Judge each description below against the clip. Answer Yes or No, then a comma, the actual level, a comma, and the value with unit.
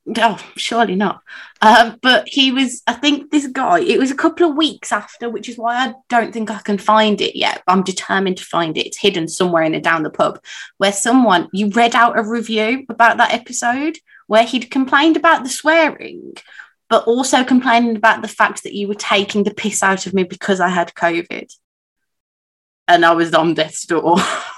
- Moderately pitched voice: No, high, 225 Hz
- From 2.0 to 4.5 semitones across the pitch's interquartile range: No, average, 5.0 semitones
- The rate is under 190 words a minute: No, fast, 205 wpm